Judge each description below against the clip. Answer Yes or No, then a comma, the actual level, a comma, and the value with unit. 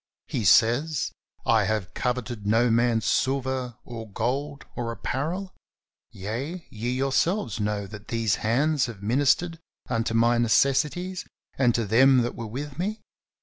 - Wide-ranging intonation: No, average, 3.8 semitones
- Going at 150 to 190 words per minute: No, average, 140 wpm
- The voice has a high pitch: No, low, 120 Hz